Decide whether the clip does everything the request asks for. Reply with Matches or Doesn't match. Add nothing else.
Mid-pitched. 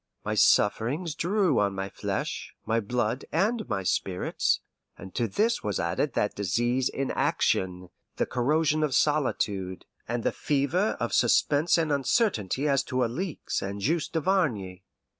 Doesn't match